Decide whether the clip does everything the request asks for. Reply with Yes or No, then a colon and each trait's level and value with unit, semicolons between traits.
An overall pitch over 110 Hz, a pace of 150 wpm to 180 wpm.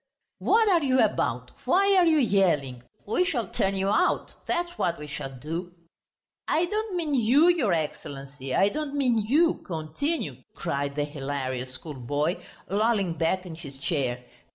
Yes: medium, 185 Hz; average, 155 wpm